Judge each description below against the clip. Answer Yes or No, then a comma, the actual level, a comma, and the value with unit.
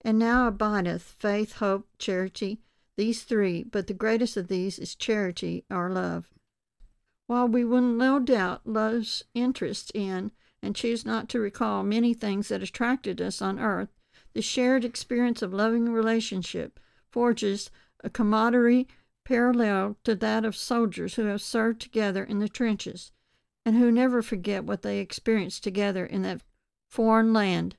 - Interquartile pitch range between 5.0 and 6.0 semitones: No, average, 2.8 semitones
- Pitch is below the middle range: No, high, 220 Hz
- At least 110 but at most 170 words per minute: Yes, average, 150 wpm